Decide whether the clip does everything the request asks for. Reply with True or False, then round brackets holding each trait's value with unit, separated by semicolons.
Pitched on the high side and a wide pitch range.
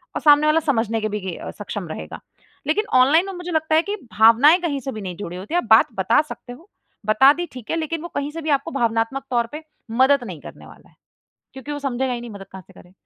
True (265 Hz; 6.1 semitones)